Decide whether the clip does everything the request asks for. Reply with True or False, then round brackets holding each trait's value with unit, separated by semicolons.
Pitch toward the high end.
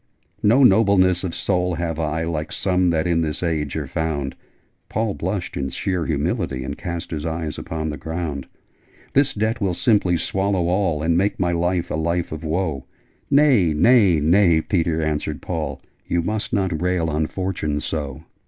False (85 Hz)